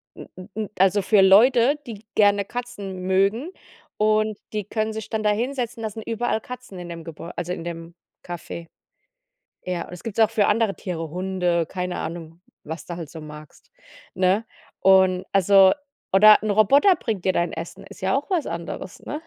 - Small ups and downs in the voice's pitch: No, average, 3.8 semitones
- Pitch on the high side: Yes, high, 195 Hz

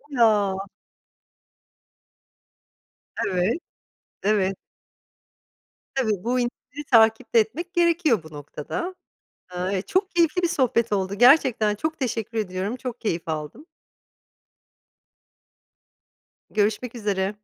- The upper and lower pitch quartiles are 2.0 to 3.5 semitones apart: No, average, 5.2 semitones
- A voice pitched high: Yes, high, 220 Hz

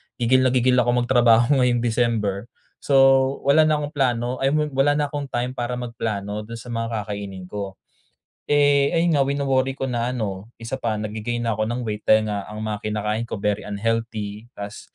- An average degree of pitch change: Yes, average, 3.5 semitones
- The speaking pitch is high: No, low, 115 Hz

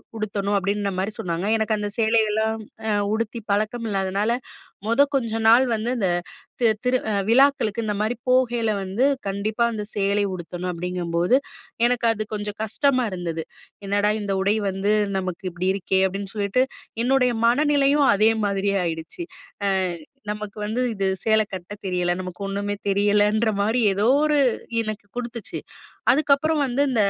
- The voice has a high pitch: Yes, high, 210 Hz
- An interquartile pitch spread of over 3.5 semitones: No, average, 3.0 semitones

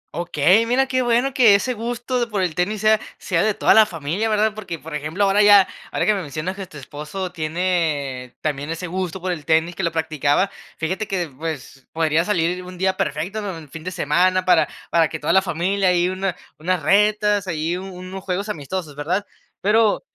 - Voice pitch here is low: No, medium, 185 Hz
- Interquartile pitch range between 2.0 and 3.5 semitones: No, average, 4.0 semitones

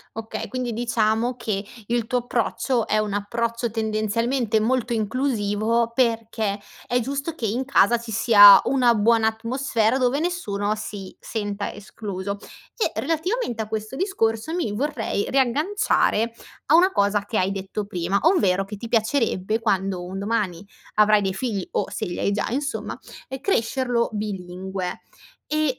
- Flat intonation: No, average, 3.5 semitones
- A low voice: No, high, 225 Hz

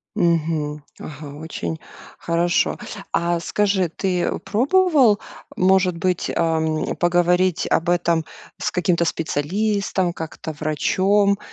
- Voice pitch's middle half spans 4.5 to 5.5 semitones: No, average, 3.1 semitones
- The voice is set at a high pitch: No, medium, 175 Hz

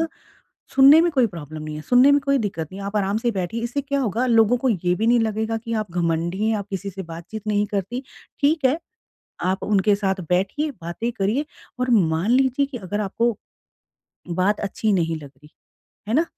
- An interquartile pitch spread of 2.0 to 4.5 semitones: No, average, 5.0 semitones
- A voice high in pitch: Yes, high, 210 Hz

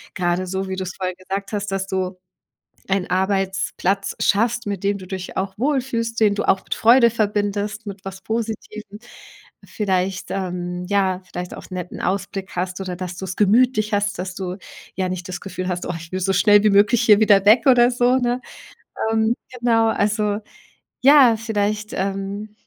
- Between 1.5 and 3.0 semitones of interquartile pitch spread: Yes, narrow, 2.5 semitones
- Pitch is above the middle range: Yes, high, 200 Hz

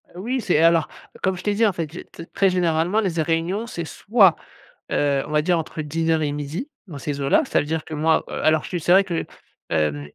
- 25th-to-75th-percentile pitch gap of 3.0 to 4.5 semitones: Yes, average, 3.5 semitones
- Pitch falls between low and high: Yes, medium, 165 Hz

